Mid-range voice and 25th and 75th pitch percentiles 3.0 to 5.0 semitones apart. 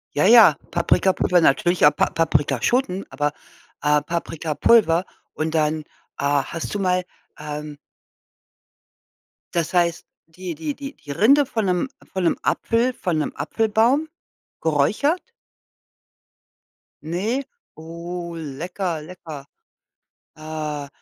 Yes: medium, 170 Hz; average, 4.1 semitones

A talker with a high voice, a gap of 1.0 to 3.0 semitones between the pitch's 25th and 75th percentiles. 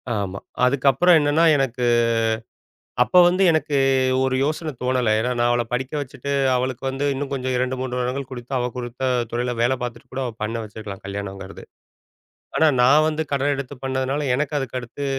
No: low, 130 Hz; narrow, 2.6 semitones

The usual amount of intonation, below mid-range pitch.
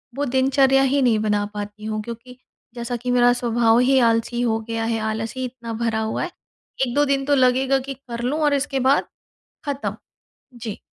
No: average, 3.1 semitones; high, 245 Hz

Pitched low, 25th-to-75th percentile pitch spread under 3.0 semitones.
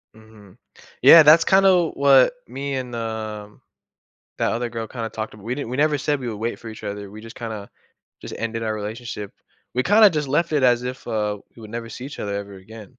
No: low, 115 Hz; average, 4.1 semitones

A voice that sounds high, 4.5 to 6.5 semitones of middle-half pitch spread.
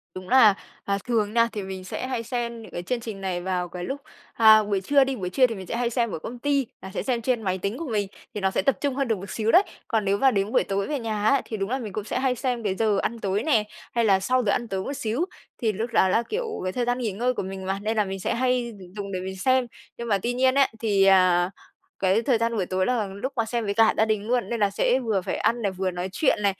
No: high, 220 Hz; average, 4.0 semitones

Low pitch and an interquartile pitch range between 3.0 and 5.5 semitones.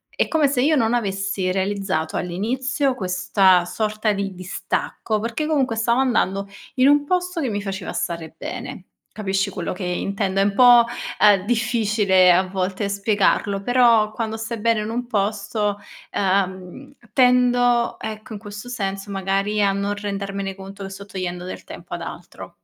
No: high, 205 Hz; average, 3.3 semitones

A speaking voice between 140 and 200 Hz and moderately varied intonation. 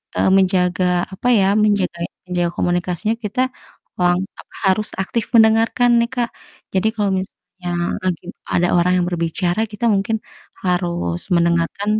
Yes: medium, 185 Hz; average, 3.2 semitones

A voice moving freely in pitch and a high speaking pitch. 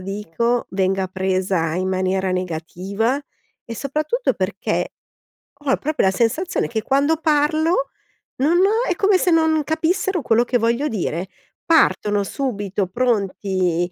Yes: wide, 8.4 semitones; high, 230 Hz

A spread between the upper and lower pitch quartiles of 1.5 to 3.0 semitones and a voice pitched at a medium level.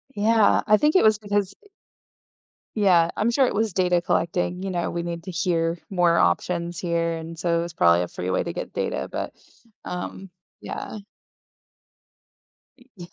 No: average, 3.4 semitones; medium, 175 Hz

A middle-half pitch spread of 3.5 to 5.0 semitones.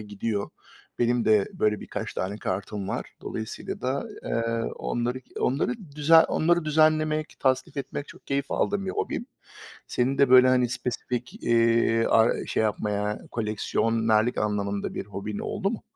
Yes: average, 4.4 semitones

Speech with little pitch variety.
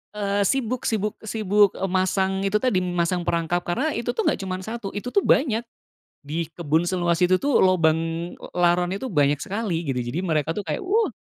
No: average, 4.0 semitones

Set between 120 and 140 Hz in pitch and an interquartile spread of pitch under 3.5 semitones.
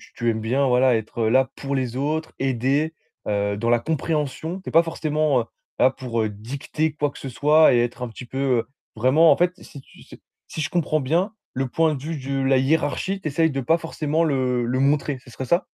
No: low, 135 Hz; average, 4.0 semitones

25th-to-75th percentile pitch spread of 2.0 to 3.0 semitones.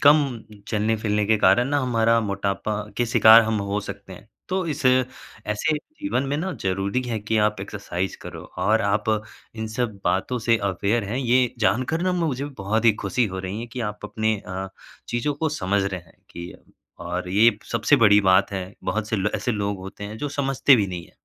No: average, 3.9 semitones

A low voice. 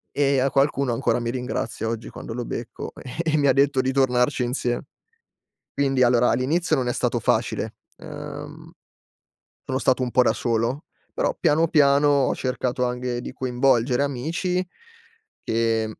Yes: low, 130 Hz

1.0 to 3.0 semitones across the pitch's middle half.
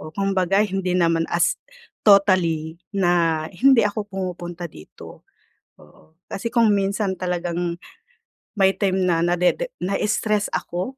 Yes: narrow, 2.6 semitones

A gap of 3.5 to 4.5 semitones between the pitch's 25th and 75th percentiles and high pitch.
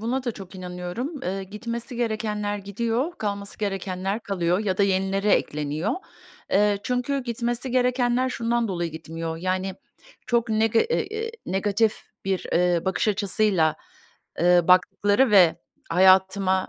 Yes: average, 4.0 semitones; high, 200 Hz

